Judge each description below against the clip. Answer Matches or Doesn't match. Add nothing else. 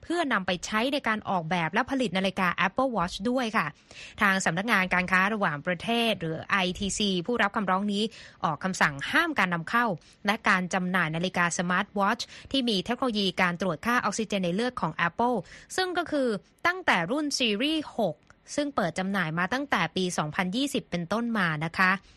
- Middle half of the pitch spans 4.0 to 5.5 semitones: Matches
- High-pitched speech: Matches